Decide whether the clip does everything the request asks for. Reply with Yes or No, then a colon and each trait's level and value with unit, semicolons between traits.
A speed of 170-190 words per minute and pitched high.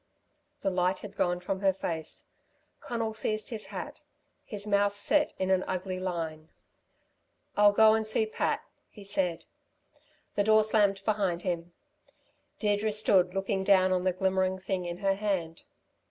No: average, 155 wpm; high, 195 Hz